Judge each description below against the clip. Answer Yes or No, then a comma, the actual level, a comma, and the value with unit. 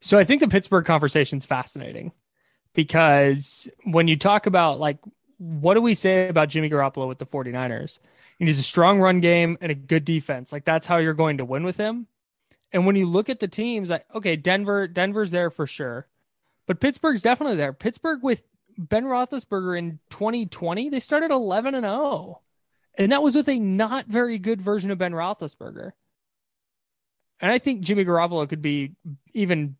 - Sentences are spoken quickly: No, average, 185 wpm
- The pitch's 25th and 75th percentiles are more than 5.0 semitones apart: Yes, wide, 5.5 semitones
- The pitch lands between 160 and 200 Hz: Yes, medium, 185 Hz